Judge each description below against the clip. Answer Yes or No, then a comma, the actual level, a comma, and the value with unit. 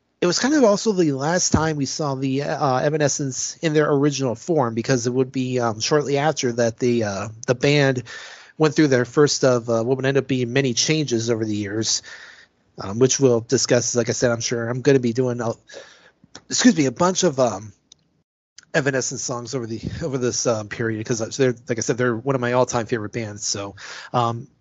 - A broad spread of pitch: No, average, 3.5 semitones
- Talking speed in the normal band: No, fast, 215 wpm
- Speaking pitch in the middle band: No, low, 130 Hz